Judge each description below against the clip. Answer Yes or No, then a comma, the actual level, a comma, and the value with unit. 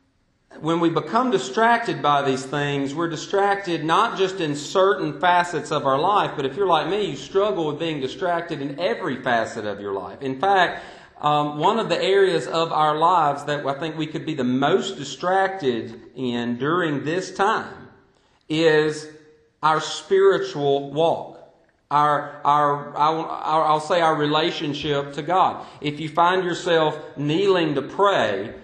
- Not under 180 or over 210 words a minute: No, average, 155 wpm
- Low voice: No, medium, 155 Hz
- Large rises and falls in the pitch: No, average, 2.9 semitones